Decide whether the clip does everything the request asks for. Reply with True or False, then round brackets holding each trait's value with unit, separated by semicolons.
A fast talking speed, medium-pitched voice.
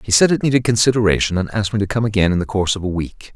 False (305 wpm; 105 Hz)